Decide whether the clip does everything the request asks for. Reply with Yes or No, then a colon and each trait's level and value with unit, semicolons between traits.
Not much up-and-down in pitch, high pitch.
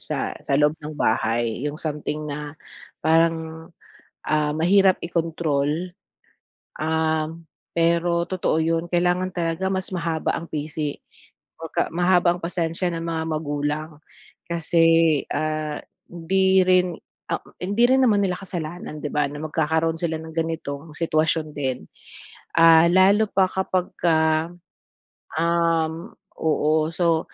No: narrow, 2.1 semitones; medium, 165 Hz